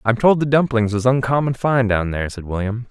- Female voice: No, male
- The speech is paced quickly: Yes, fast, 225 wpm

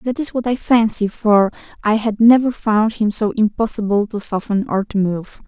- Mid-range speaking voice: No, high, 215 Hz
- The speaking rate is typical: Yes, average, 195 wpm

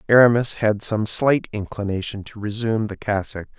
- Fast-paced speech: No, average, 150 wpm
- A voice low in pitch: Yes, low, 105 Hz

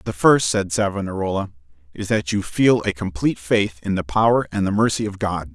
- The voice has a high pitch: No, very low, 95 Hz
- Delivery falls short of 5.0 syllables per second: No, 5.5 syllables/s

